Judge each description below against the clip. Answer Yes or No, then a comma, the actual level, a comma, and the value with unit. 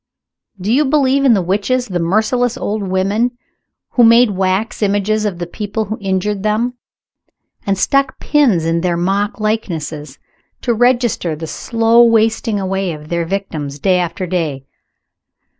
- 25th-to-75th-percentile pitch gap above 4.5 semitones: No, average, 4.2 semitones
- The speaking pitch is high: Yes, high, 205 Hz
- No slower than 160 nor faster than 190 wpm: No, average, 150 wpm